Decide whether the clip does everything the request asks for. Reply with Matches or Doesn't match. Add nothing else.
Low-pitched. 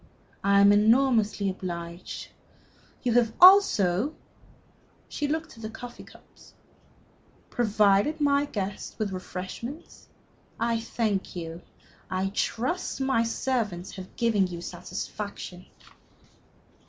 Doesn't match